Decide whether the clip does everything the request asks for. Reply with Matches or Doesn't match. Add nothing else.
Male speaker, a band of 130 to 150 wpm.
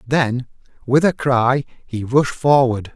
Matches